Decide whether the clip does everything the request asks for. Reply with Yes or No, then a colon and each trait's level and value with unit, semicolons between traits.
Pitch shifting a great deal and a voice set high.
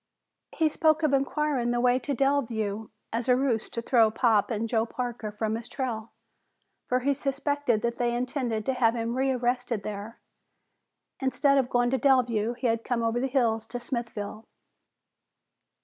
No: average, 2.7 semitones; high, 240 Hz